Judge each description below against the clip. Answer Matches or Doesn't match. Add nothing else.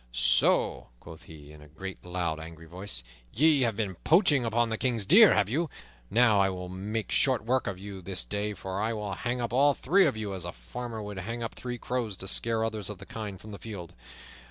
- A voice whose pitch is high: Doesn't match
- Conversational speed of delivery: Doesn't match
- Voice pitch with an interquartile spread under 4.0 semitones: Doesn't match